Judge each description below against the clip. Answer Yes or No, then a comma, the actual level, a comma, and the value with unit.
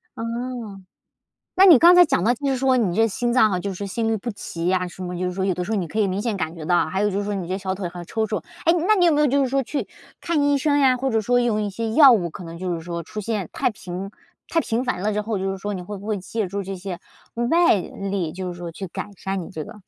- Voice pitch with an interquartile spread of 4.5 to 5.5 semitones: Yes, average, 4.9 semitones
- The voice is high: Yes, high, 205 Hz